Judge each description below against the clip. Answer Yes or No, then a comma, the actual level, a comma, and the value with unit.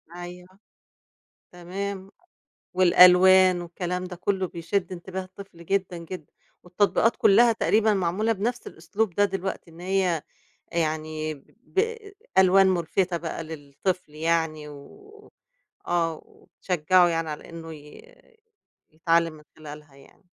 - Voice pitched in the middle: Yes, medium, 180 Hz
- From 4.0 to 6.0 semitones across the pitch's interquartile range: No, average, 2.9 semitones